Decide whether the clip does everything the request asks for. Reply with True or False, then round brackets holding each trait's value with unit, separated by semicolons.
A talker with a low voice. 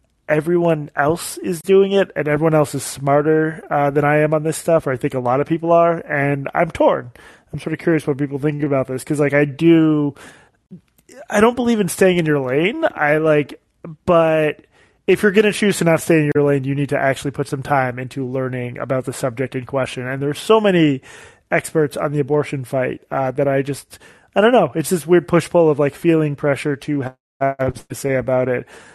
False (150 Hz)